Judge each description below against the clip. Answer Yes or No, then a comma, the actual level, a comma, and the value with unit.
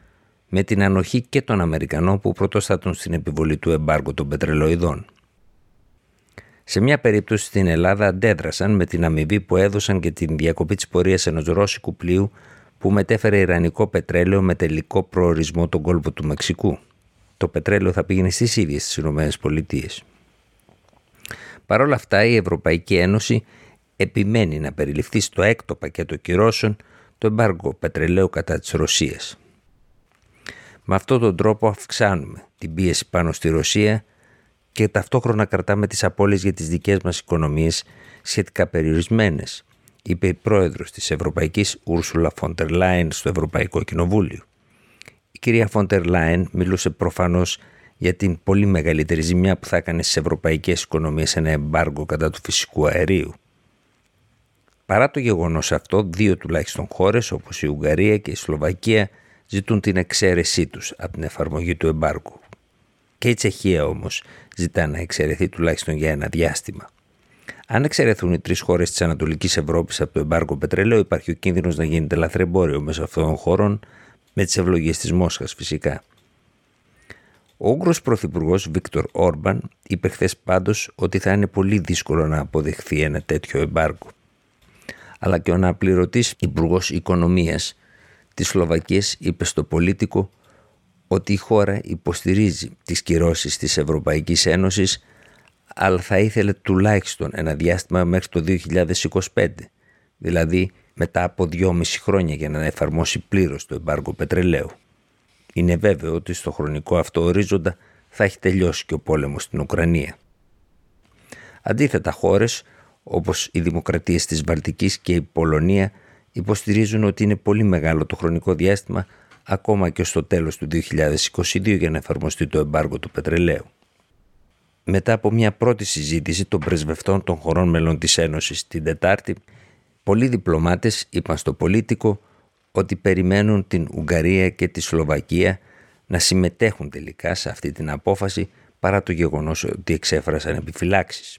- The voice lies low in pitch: Yes, very low, 90 Hz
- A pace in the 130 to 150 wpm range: Yes, average, 140 wpm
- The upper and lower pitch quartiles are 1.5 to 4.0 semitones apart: Yes, average, 3.6 semitones